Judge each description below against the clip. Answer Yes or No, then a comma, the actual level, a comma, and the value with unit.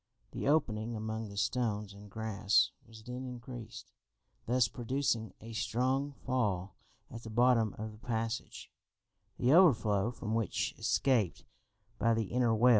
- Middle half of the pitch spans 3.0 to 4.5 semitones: No, narrow, 2.4 semitones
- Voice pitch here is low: Yes, low, 115 Hz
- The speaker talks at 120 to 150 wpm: Yes, average, 140 wpm